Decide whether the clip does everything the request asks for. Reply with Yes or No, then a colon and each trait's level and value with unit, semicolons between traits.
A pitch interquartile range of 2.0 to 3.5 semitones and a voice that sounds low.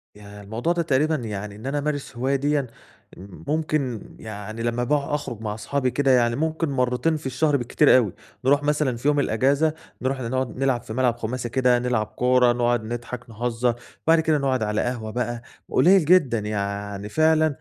No: average, 3.9 semitones; low, 125 Hz